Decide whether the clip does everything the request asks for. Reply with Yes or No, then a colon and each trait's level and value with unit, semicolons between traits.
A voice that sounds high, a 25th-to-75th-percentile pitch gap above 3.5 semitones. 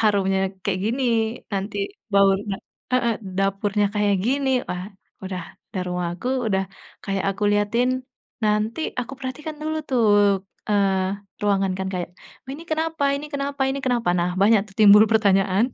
Yes: high, 205 Hz; average, 4.6 semitones